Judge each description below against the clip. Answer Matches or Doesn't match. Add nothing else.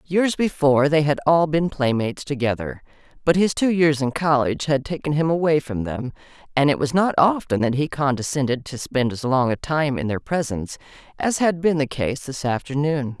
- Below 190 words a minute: Doesn't match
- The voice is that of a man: Doesn't match